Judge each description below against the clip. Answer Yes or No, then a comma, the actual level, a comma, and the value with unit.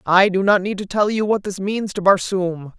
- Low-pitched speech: No, high, 195 Hz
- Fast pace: Yes, fast, 260 wpm